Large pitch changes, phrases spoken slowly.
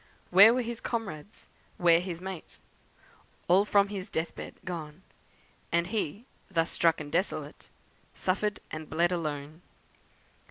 No: average, 3.6 semitones; slow, 130 wpm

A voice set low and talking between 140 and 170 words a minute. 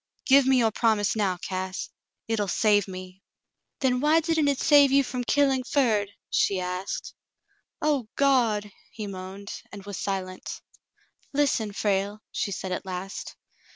No: high, 210 Hz; average, 150 wpm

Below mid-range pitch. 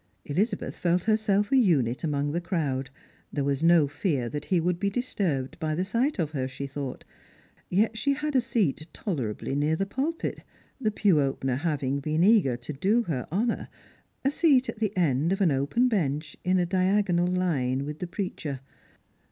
No: medium, 170 Hz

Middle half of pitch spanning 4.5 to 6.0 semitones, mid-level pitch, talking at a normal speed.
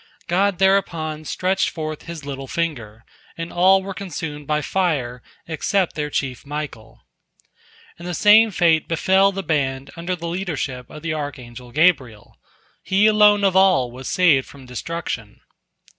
Yes: wide, 5.4 semitones; medium, 160 Hz; average, 145 wpm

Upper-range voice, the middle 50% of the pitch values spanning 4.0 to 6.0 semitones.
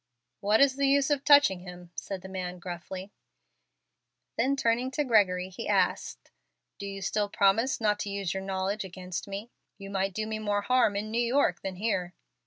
No: high, 200 Hz; average, 3.4 semitones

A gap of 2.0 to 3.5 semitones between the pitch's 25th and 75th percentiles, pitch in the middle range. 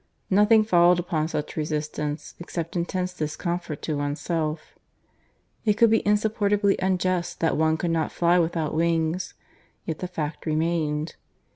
Yes: average, 2.8 semitones; medium, 170 Hz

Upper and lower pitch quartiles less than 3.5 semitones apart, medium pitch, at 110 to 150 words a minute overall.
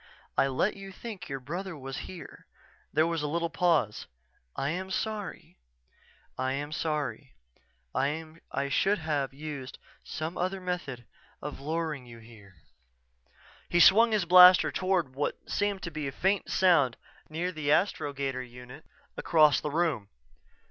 No: average, 4.9 semitones; medium, 155 Hz; average, 140 wpm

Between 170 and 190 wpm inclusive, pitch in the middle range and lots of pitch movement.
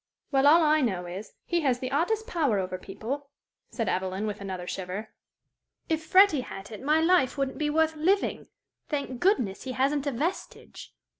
No: average, 175 wpm; very high, 275 Hz; wide, 7.3 semitones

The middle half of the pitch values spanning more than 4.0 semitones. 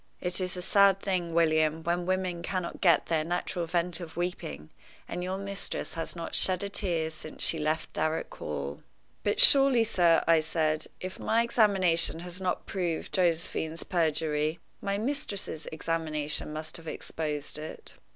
No: average, 2.8 semitones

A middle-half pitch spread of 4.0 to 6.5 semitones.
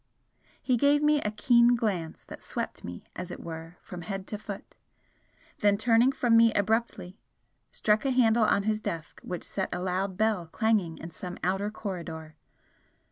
Yes: average, 4.3 semitones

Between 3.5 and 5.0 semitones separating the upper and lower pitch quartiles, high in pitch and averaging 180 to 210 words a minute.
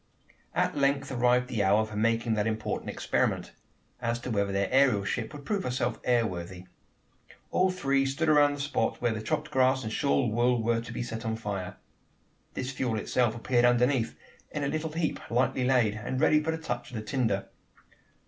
No: average, 3.8 semitones; low, 120 Hz; average, 195 wpm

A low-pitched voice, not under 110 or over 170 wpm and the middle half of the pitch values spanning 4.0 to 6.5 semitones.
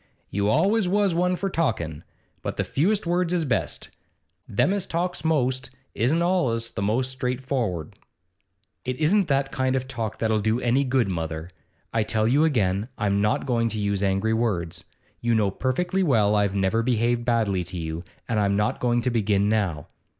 No: low, 115 Hz; average, 180 wpm; wide, 5.6 semitones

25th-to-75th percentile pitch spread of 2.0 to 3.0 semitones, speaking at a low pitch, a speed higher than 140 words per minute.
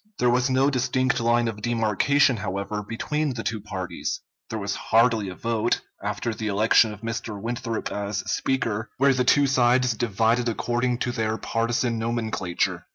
Yes: narrow, 2.4 semitones; low, 115 Hz; average, 160 wpm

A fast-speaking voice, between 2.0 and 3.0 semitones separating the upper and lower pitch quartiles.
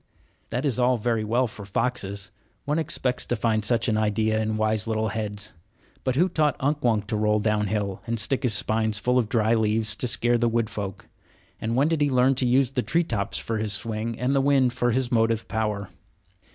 Yes: fast, 215 wpm; average, 2.7 semitones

